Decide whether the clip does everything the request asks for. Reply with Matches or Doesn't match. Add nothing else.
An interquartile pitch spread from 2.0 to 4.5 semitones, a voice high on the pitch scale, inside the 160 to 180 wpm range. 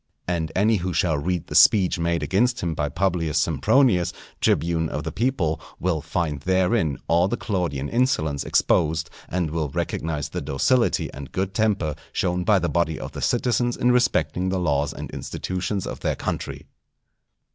Doesn't match